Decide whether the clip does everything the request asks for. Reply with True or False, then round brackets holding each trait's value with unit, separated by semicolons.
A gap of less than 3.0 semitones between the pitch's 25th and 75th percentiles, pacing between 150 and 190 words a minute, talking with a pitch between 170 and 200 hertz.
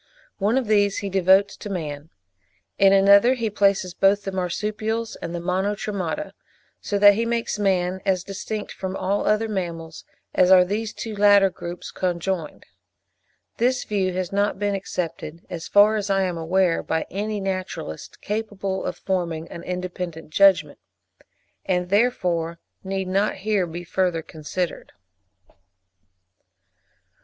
False (2.5 semitones; 140 wpm; 190 Hz)